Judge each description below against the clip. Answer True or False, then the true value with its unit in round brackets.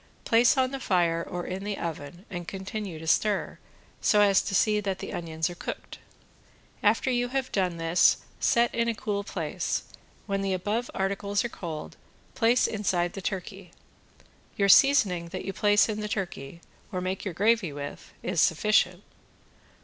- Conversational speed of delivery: True (170 wpm)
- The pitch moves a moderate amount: True (3.4 semitones)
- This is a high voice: True (195 Hz)